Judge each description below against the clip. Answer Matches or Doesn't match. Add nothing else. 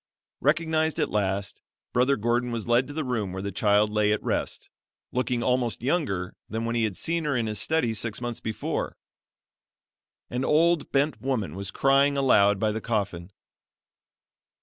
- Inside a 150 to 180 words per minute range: Matches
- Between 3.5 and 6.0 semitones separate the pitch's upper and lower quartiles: Matches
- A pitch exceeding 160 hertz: Doesn't match